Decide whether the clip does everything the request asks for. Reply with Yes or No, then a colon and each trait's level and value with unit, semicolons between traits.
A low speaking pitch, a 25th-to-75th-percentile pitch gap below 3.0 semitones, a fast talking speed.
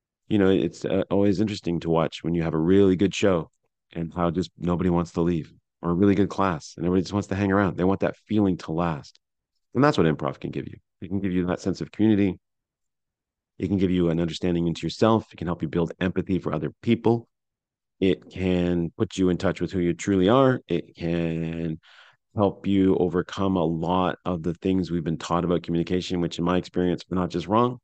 Yes: very low, 90 Hz; narrow, 2.4 semitones; fast, 230 wpm